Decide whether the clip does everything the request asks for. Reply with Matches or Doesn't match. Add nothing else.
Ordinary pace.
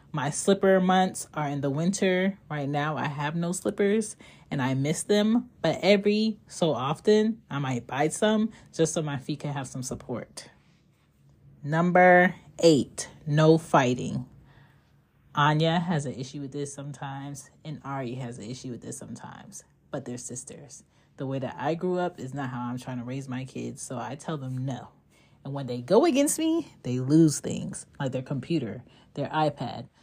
Matches